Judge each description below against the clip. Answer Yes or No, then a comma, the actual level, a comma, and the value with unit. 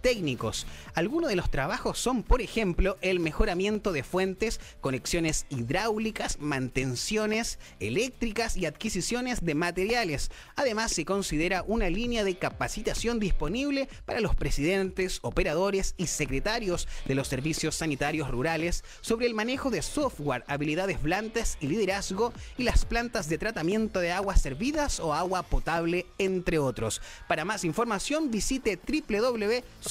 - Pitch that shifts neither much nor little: No, wide, 6.3 semitones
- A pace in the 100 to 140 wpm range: Yes, average, 130 wpm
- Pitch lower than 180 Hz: No, high, 190 Hz